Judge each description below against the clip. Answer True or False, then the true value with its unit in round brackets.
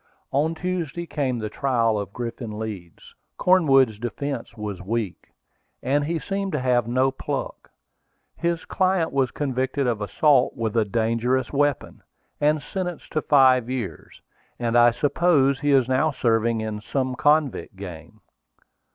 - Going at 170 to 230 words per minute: False (145 wpm)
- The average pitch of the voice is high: False (130 Hz)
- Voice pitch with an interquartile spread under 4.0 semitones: False (4.3 semitones)